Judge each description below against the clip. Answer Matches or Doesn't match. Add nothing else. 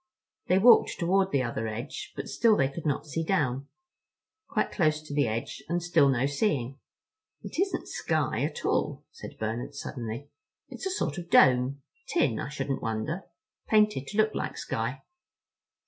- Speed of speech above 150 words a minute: Matches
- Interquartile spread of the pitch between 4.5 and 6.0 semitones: Matches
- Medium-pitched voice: Matches